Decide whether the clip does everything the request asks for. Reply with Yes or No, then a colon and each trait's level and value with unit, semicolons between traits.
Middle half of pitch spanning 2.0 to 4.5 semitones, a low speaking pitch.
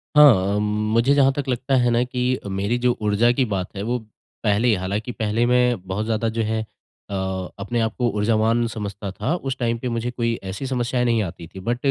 Yes: average, 2.9 semitones; low, 115 Hz